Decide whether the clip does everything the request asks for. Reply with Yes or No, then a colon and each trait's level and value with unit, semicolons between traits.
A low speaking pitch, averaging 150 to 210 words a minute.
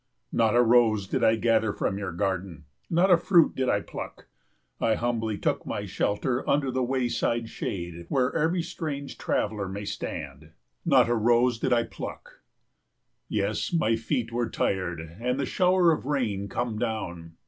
Yes: low, 115 Hz; average, 165 wpm